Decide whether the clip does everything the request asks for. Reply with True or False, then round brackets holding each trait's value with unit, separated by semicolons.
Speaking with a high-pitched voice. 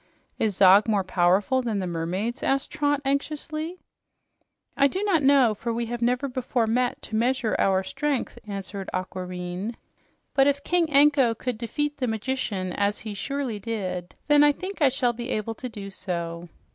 True (235 Hz)